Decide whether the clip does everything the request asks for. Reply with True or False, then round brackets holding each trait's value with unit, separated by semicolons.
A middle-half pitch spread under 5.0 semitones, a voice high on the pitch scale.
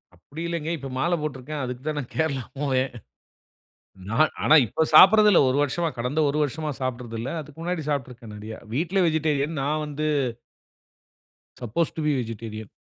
False (4.0 semitones; 145 Hz)